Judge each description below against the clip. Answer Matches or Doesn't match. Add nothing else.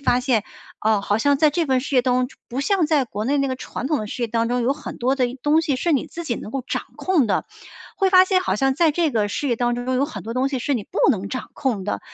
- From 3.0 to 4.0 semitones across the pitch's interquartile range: Matches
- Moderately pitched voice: Doesn't match